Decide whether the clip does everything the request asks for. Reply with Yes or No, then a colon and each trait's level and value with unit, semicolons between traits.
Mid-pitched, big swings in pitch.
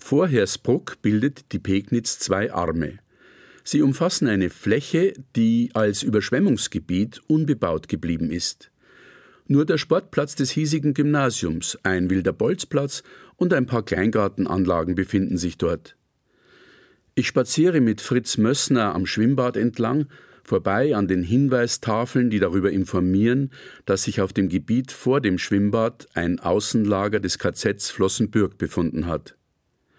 No: low, 110 Hz; wide, 5.7 semitones